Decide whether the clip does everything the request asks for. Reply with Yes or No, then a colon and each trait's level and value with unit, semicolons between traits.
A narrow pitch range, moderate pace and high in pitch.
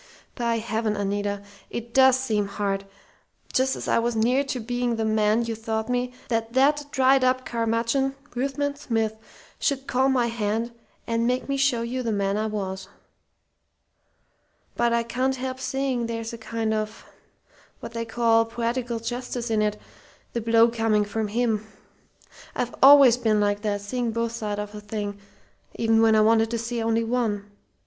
Yes: narrow, 2.3 semitones; average, 170 wpm; high, 230 Hz